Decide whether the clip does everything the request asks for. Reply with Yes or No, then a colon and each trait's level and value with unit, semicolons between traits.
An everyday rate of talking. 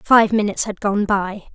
Yes: average, 195 wpm